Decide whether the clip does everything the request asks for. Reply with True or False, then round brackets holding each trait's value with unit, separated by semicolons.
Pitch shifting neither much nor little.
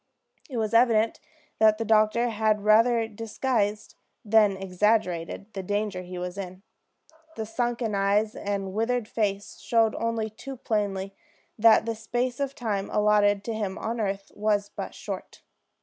False (2.2 semitones)